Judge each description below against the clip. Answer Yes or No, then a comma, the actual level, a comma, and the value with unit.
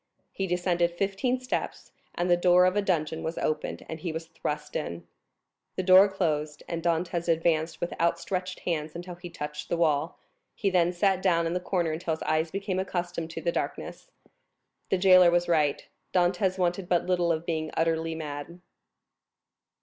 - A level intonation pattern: Yes, narrow, 2.2 semitones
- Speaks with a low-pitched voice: No, medium, 175 Hz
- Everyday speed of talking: Yes, average, 175 wpm